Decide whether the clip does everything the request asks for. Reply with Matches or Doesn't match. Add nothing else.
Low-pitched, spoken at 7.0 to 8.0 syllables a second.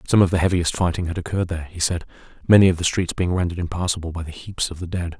Matches